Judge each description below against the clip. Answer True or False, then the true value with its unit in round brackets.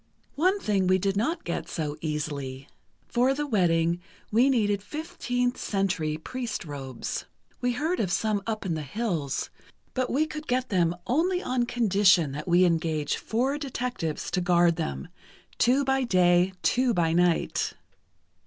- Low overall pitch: False (195 Hz)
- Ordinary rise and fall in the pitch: False (7.1 semitones)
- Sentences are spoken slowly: False (155 wpm)